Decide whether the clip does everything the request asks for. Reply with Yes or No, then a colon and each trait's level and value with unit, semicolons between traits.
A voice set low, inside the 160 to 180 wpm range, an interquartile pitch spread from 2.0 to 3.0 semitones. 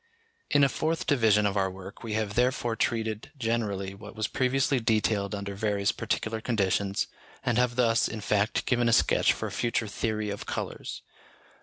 Yes: low, 110 Hz; average, 175 wpm; average, 2.7 semitones